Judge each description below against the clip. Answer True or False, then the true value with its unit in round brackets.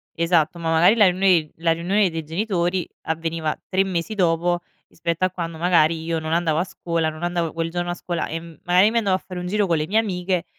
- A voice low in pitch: False (175 Hz)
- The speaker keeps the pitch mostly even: True (2.1 semitones)